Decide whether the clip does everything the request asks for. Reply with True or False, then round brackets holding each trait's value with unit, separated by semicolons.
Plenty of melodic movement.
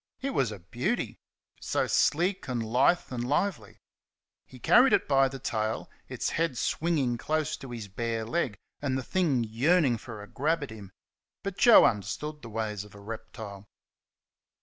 True (5.9 semitones)